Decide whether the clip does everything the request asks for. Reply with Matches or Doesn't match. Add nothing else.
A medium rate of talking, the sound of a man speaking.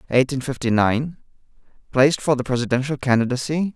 Doesn't match